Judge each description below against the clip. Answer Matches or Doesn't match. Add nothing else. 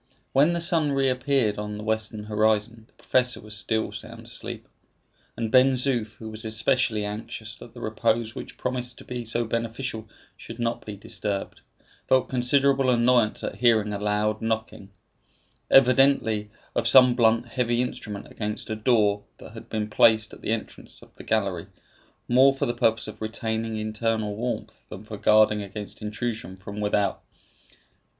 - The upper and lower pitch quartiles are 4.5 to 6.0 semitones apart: Doesn't match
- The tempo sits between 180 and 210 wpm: Doesn't match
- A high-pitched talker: Doesn't match